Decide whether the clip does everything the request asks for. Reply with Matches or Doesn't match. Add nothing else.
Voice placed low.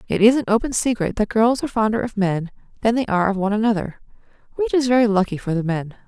Doesn't match